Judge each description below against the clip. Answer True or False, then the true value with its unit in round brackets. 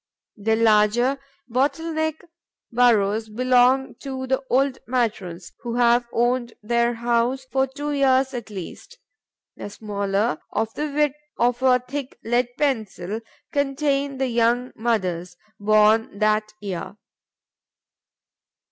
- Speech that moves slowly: True (120 wpm)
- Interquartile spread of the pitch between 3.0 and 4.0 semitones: True (3.7 semitones)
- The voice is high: True (240 Hz)